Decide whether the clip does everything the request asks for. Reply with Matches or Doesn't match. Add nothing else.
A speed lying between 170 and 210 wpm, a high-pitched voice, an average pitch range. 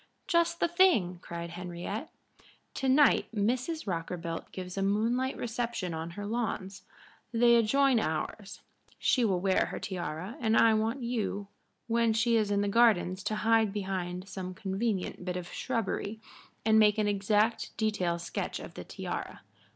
Doesn't match